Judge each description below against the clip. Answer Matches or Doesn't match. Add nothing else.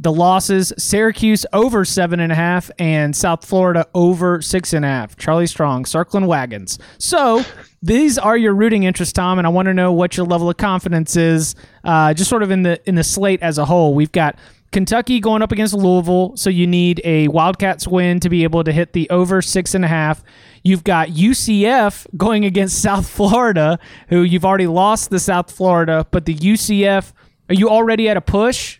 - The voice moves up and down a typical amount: Matches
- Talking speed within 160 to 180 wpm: Doesn't match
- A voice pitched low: Doesn't match